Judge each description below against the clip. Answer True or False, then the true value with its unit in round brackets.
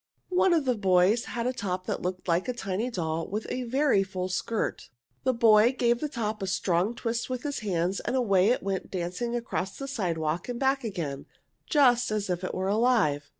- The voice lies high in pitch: True (215 Hz)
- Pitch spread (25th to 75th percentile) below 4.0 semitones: False (5.1 semitones)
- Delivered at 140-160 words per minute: False (205 wpm)